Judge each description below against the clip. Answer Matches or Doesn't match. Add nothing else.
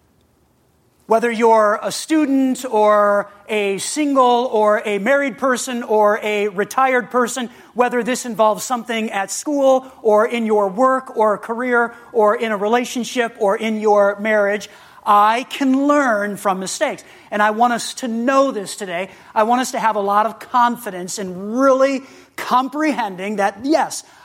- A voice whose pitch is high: Matches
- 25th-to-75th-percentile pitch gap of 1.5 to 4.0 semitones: Matches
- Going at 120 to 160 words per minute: Matches